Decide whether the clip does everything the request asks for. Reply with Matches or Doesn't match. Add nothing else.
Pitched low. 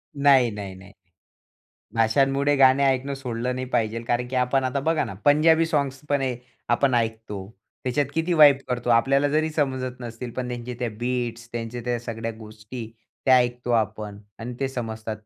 Matches